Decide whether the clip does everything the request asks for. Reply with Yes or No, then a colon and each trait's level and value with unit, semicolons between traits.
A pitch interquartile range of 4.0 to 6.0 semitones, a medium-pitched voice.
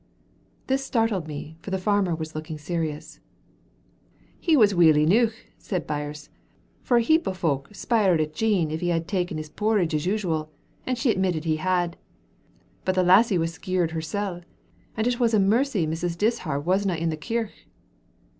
Yes: average, 5.1 semitones; medium, 180 Hz